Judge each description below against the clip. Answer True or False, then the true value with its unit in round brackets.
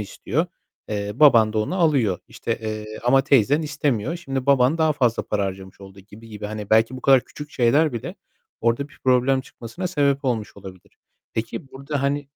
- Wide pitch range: False (4.6 semitones)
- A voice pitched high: False (125 Hz)